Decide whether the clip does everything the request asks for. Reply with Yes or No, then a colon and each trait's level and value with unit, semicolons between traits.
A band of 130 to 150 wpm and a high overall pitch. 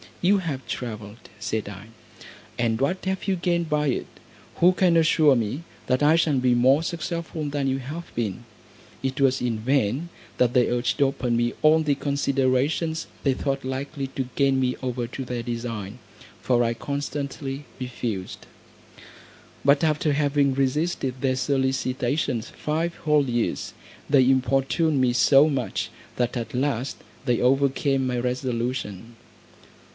No: average, 145 wpm; low, 135 Hz